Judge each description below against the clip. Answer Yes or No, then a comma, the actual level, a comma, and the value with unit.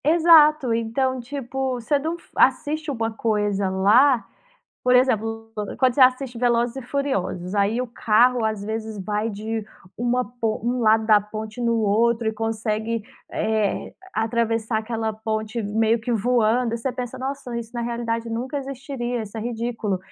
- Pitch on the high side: Yes, high, 230 Hz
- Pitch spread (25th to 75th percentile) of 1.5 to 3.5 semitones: Yes, narrow, 2.4 semitones